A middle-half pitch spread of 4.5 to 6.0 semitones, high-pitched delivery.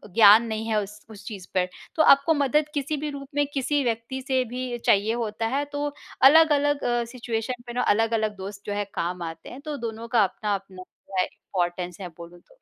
Yes: wide, 5.5 semitones; high, 225 Hz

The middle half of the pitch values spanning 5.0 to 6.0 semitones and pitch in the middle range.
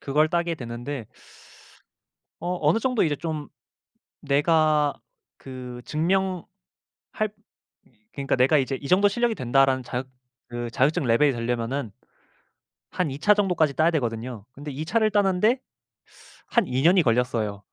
Yes: wide, 5.6 semitones; medium, 145 Hz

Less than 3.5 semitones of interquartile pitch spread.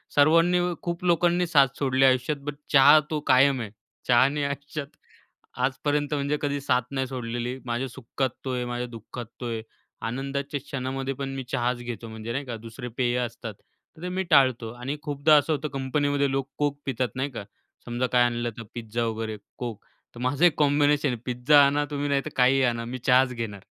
Yes: average, 2.9 semitones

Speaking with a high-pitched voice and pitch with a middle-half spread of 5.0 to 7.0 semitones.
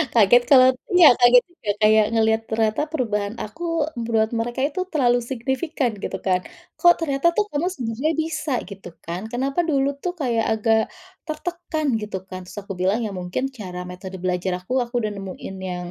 Yes: high, 230 Hz; wide, 5.4 semitones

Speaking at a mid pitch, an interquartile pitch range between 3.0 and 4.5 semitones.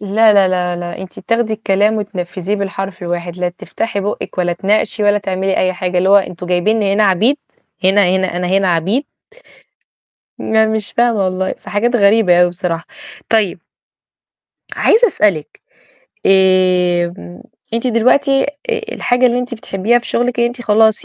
No: high, 200 Hz; average, 3.6 semitones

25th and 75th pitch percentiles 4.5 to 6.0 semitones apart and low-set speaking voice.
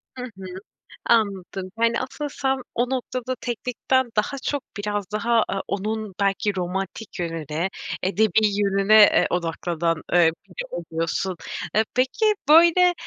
No: average, 5.1 semitones; high, 210 Hz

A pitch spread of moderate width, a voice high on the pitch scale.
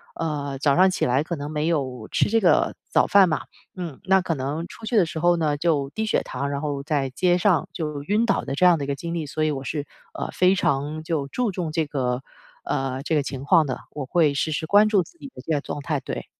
No: average, 3.9 semitones; medium, 155 Hz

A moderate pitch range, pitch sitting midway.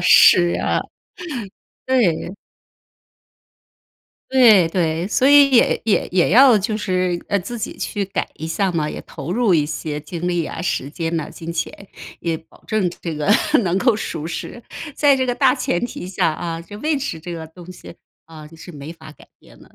Yes: average, 4.8 semitones; medium, 180 Hz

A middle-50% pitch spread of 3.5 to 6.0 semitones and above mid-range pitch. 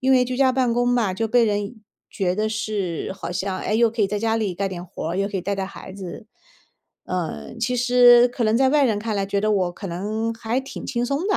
Yes: average, 3.9 semitones; high, 215 Hz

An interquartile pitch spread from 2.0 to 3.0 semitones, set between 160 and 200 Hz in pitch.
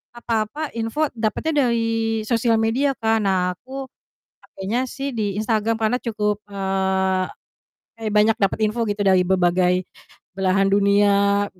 No: average, 2.7 semitones; high, 215 Hz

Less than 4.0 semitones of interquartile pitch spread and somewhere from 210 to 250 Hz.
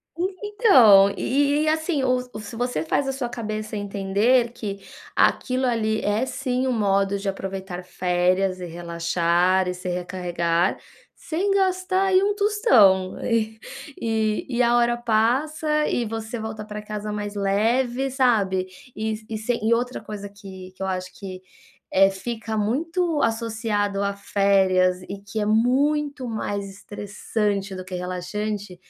No: average, 4.4 semitones; high, 215 Hz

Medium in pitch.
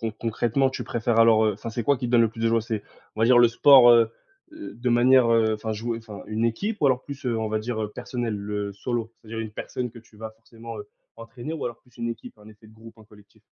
No: low, 115 Hz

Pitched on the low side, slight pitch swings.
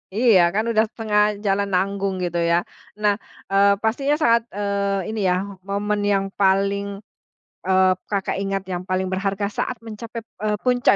No: high, 200 Hz; narrow, 1.9 semitones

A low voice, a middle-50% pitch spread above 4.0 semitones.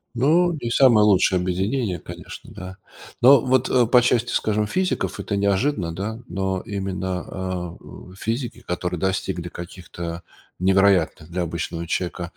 Yes: very low, 95 Hz; average, 4.5 semitones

